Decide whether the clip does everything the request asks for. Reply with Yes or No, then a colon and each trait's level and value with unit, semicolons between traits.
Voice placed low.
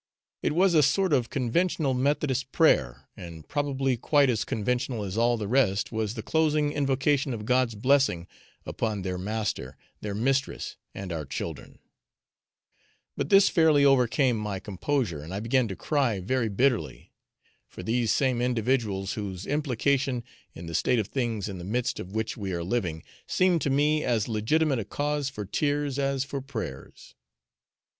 Yes: low, 125 Hz